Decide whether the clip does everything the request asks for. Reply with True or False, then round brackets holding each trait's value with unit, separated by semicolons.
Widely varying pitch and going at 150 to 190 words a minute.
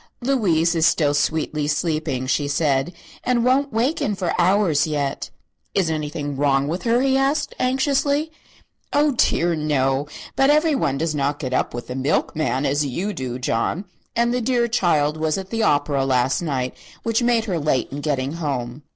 True (8.3 semitones; 170 wpm)